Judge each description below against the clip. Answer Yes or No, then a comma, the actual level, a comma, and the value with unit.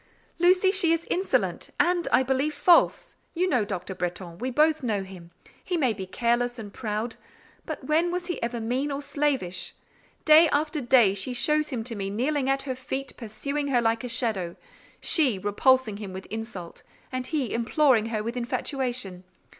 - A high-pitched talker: Yes, very high, 250 Hz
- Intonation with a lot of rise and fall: Yes, wide, 5.7 semitones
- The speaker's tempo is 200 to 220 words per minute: No, average, 175 wpm